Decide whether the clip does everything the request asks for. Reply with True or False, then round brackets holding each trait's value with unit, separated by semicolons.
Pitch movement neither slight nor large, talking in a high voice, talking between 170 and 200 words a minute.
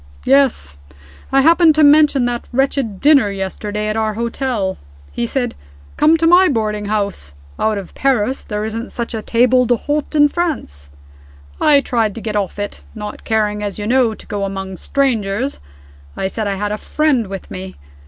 True (4.7 semitones; 225 Hz; 175 wpm)